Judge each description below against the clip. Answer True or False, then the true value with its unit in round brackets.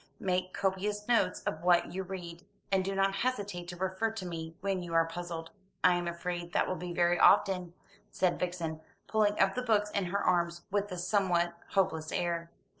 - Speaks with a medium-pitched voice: True (180 Hz)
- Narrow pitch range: True (2.1 semitones)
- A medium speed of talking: True (190 wpm)